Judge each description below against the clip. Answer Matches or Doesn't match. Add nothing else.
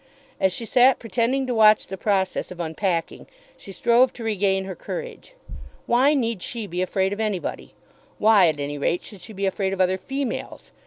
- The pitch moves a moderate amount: Matches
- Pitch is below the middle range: Doesn't match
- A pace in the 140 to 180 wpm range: Doesn't match